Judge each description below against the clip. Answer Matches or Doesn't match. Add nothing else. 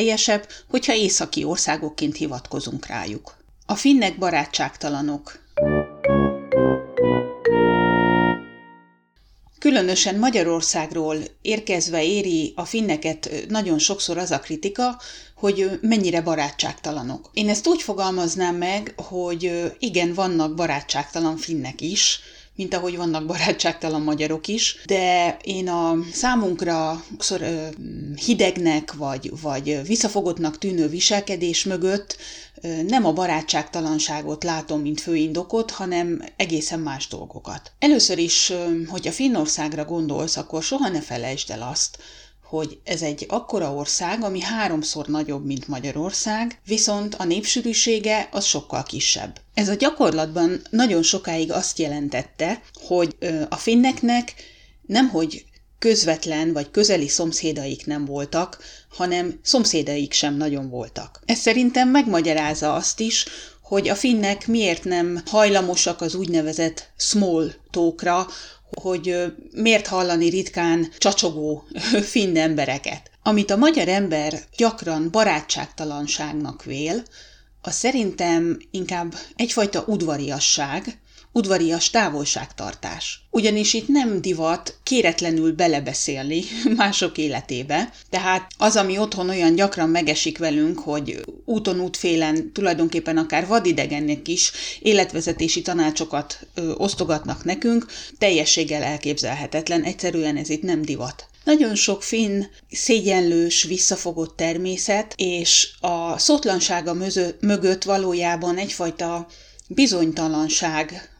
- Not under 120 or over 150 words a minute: Doesn't match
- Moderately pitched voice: Matches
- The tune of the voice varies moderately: Matches